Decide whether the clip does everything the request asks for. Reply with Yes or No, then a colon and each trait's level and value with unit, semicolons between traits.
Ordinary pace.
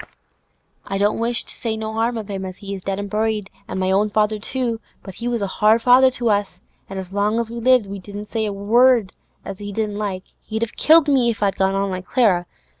No: fast, 250 wpm